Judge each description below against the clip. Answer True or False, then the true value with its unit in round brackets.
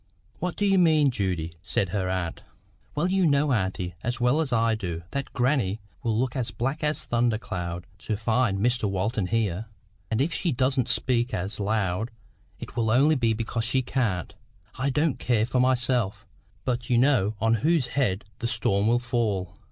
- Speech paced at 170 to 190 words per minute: True (185 wpm)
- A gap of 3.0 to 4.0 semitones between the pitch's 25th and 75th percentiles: False (4.4 semitones)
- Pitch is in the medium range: False (115 Hz)